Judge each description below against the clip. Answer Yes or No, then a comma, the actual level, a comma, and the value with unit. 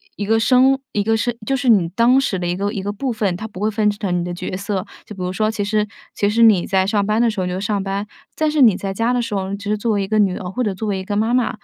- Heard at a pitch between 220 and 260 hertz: No, high, 205 Hz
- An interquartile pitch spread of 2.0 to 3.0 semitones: Yes, narrow, 2.6 semitones